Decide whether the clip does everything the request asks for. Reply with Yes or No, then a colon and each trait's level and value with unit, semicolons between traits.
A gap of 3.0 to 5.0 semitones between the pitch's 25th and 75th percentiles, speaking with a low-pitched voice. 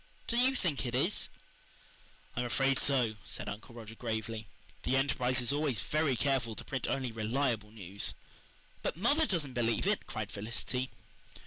Yes: average, 4.1 semitones; low, 125 Hz